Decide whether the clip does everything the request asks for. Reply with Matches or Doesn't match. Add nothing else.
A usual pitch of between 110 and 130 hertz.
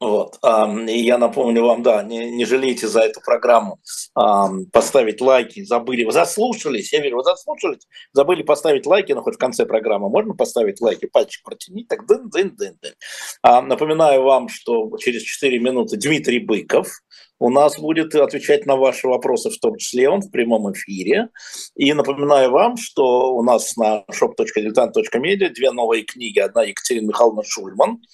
Doesn't match